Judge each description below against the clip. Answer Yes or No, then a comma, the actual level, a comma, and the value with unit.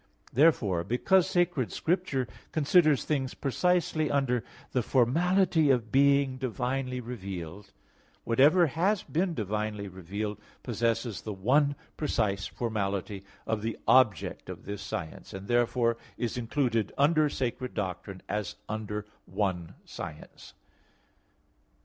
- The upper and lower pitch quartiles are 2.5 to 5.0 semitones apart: No, wide, 5.5 semitones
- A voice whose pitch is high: No, low, 120 Hz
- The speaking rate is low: Yes, slow, 115 wpm